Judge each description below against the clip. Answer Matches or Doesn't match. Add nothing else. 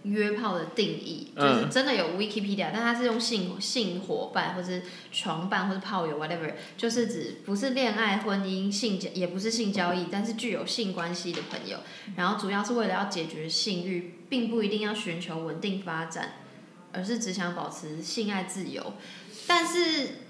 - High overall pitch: Matches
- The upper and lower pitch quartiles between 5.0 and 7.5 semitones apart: Doesn't match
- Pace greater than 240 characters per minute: Matches